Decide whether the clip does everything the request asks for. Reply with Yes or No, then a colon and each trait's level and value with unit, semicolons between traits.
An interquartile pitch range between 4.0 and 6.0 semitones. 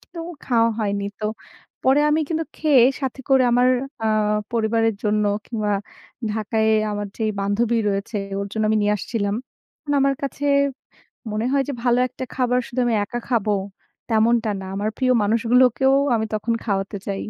No: average, 3.2 semitones